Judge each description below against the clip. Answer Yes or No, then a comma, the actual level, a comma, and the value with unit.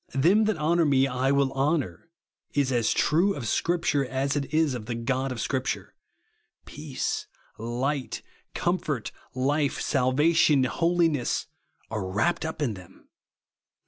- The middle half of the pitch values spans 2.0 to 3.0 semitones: No, average, 3.6 semitones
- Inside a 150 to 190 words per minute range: No, average, 140 wpm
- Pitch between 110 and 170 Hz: Yes, medium, 140 Hz